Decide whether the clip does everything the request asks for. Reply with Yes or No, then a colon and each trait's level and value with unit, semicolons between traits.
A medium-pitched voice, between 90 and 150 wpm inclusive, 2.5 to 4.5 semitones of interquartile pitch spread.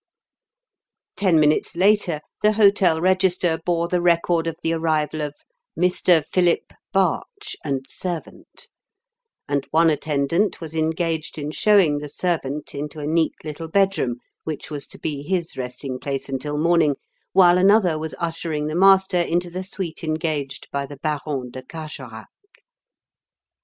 Yes: medium, 160 Hz; average, 140 wpm; average, 3.3 semitones